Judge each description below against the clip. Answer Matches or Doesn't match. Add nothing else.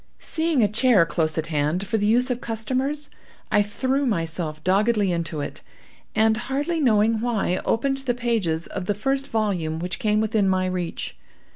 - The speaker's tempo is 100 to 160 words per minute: Doesn't match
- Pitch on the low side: Doesn't match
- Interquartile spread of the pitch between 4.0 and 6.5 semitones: Matches